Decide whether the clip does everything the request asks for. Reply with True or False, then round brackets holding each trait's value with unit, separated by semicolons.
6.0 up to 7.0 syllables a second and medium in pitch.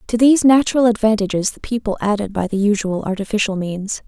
False (6.1 syllables/s; 215 Hz)